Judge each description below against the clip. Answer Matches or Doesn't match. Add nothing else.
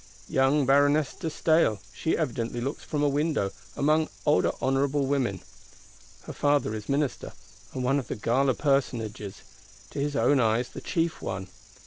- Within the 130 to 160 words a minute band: Matches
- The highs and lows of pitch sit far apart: Doesn't match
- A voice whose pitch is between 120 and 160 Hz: Matches